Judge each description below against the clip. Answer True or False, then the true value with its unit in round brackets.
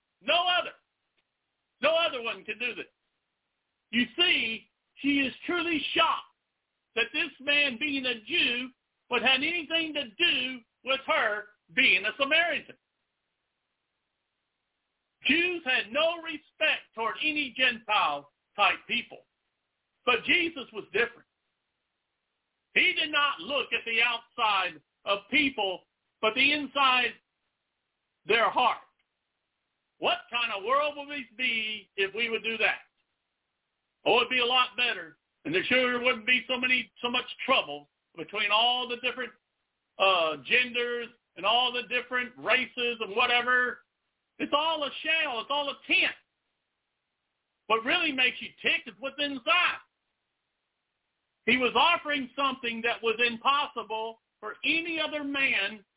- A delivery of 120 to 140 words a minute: True (135 wpm)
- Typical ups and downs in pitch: True (4.3 semitones)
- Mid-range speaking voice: False (255 Hz)